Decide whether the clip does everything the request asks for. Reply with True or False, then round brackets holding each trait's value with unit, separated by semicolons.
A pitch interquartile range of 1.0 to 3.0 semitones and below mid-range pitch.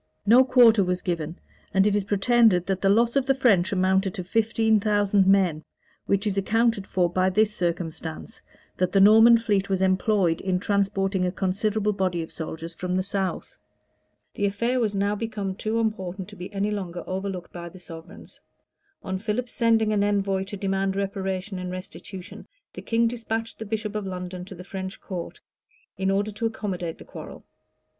False (2.6 semitones; 195 Hz)